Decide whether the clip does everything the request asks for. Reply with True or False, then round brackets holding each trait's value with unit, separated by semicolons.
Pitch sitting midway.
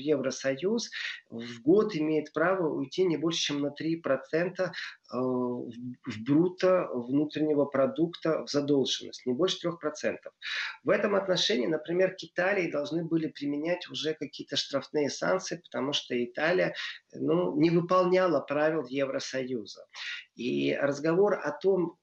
True (155 Hz)